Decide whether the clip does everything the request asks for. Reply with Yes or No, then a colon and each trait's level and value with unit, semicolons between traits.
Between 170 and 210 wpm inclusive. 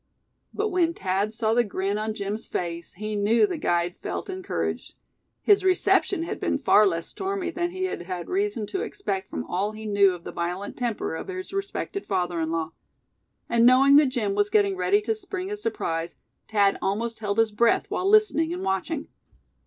Yes: average, 190 wpm